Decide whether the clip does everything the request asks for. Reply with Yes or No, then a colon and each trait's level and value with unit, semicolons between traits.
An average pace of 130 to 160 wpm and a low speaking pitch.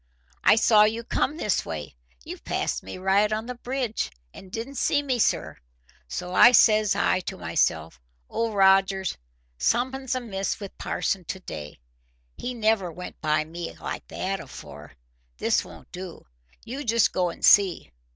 No: average, 155 wpm; high, 200 Hz